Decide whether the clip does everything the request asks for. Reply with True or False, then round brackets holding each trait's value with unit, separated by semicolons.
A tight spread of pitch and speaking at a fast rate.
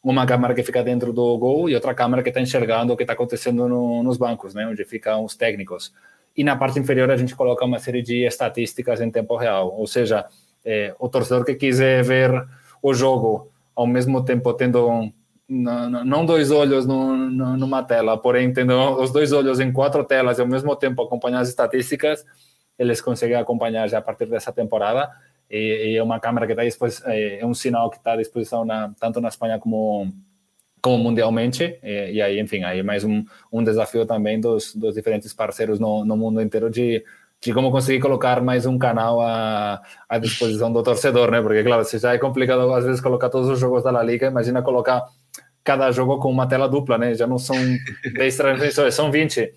True (2.3 semitones; 205 wpm)